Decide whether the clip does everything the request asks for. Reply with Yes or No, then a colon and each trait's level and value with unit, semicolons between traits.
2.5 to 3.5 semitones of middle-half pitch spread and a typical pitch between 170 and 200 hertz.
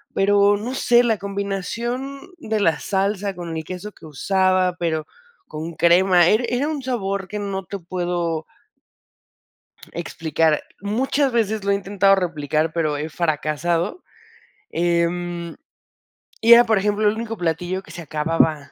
No: average, 3.9 semitones; medium, 185 Hz